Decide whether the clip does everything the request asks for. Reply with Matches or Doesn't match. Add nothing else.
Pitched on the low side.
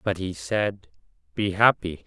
Matches